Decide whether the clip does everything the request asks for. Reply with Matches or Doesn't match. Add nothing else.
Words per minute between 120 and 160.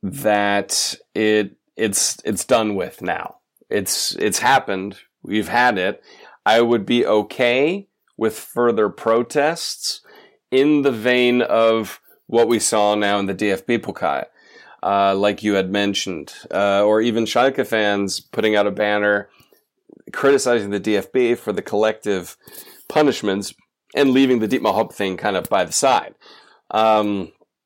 Matches